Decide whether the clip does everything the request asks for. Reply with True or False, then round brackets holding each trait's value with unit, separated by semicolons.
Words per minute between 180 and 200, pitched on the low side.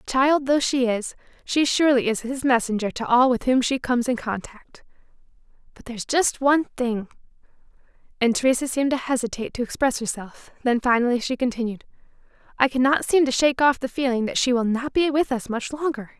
False (185 wpm; 250 Hz)